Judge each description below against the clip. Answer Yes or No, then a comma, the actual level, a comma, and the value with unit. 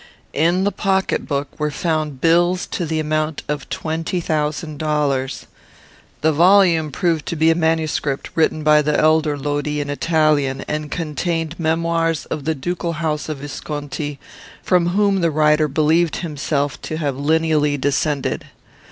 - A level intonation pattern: Yes, narrow, 1.9 semitones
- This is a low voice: No, medium, 155 Hz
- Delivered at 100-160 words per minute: Yes, average, 150 wpm